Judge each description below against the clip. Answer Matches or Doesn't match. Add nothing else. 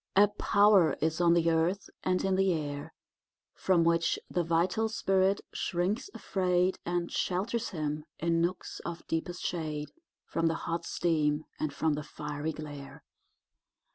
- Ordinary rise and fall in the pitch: Matches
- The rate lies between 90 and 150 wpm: Matches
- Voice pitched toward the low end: Doesn't match